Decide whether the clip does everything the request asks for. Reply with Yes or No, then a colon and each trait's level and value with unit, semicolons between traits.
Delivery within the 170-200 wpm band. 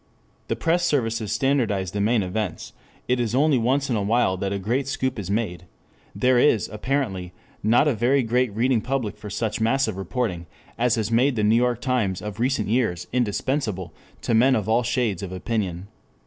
Yes: average, 190 wpm